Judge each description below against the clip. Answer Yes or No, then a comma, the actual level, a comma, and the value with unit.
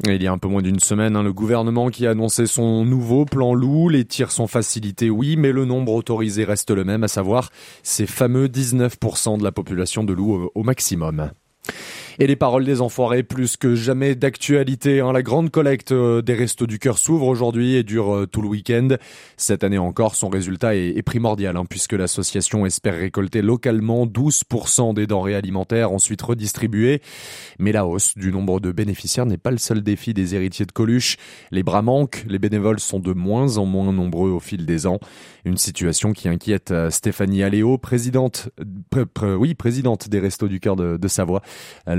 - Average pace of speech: Yes, average, 185 wpm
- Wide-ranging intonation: No, average, 4.1 semitones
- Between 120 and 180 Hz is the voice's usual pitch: No, low, 110 Hz